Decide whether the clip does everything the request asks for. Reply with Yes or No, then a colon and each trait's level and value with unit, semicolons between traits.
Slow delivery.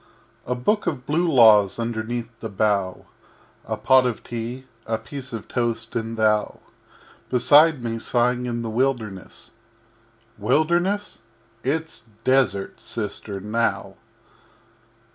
Yes: slow, 125 wpm